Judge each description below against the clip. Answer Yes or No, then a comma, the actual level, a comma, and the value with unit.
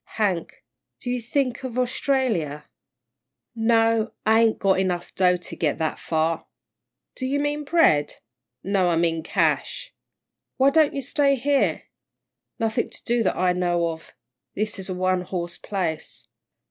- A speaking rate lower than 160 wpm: Yes, average, 150 wpm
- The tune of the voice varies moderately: No, wide, 6.3 semitones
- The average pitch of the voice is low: No, high, 200 Hz